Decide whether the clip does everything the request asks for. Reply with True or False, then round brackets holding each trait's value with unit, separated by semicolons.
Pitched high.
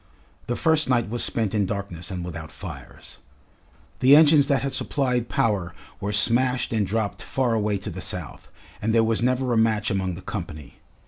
False (110 Hz)